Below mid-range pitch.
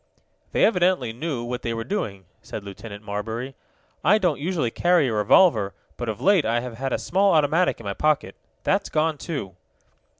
Yes: low, 130 Hz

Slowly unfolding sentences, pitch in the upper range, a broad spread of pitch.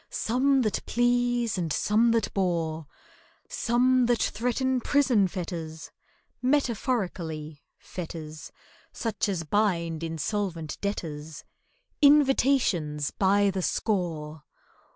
Yes: slow, 90 wpm; high, 200 Hz; wide, 6.9 semitones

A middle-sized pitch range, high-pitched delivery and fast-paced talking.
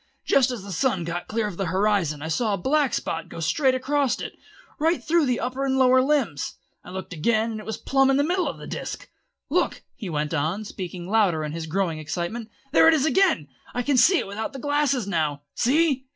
No: wide, 7.7 semitones; high, 220 Hz; fast, 225 wpm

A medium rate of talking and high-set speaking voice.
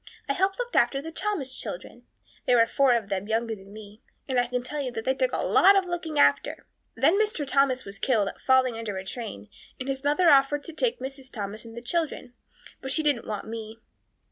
No: fast, 220 wpm; very high, 260 Hz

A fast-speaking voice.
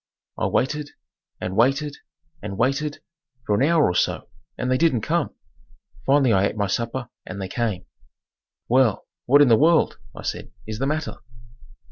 No: average, 165 wpm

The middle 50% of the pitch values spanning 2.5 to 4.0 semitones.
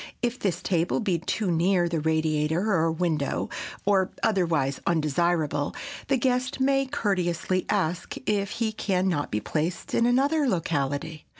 No: average, 4.9 semitones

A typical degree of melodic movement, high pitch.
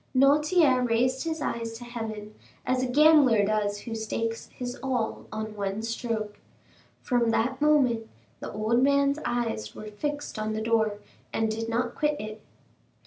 Yes: average, 3.3 semitones; high, 230 Hz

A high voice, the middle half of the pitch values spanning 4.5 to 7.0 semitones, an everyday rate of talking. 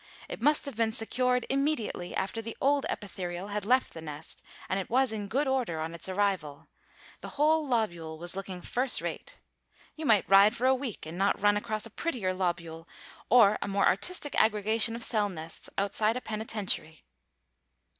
Yes: high, 210 Hz; average, 5.1 semitones; average, 180 wpm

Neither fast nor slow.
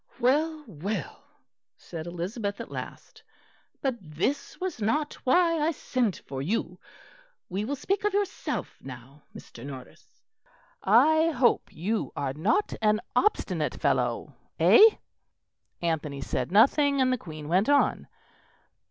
No: slow, 125 wpm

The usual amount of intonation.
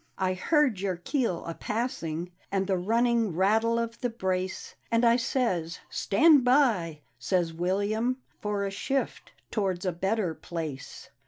Yes: average, 4.6 semitones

